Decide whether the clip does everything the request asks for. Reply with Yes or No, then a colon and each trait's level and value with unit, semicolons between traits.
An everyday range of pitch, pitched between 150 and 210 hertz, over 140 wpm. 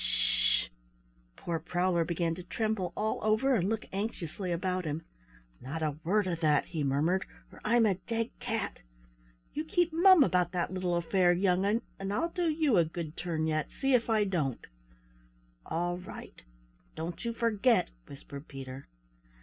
Yes: average, 5.0 semitones; medium, 185 Hz; average, 165 wpm